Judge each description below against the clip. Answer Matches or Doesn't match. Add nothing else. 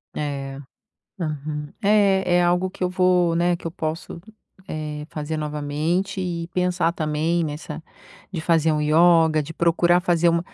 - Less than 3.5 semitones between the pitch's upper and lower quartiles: Matches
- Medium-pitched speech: Matches